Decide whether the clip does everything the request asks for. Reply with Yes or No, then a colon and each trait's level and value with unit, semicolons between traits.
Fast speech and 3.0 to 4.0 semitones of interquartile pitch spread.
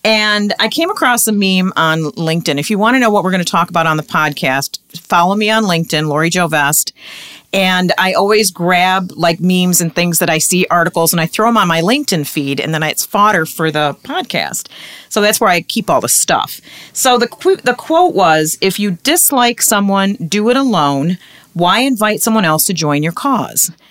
No: fast, 215 wpm; average, 5.2 semitones